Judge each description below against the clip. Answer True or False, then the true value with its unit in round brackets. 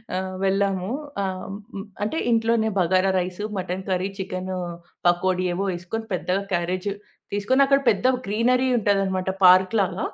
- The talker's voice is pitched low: False (190 Hz)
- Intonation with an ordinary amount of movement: False (2.0 semitones)